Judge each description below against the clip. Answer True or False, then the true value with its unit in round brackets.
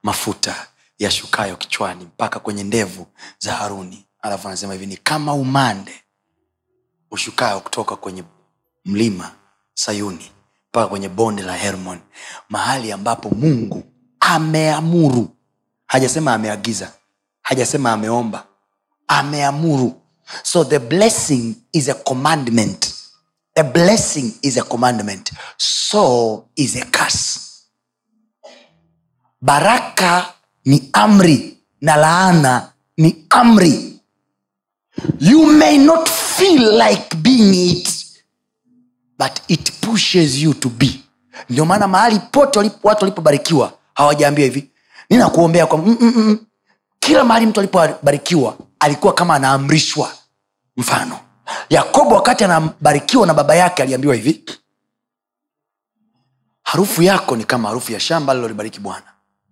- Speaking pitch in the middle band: True (150 Hz)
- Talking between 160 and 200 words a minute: False (105 wpm)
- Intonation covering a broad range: True (8.0 semitones)